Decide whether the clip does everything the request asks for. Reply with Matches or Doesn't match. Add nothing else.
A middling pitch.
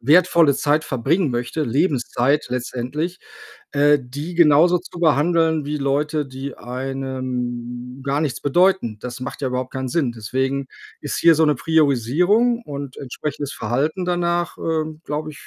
Matches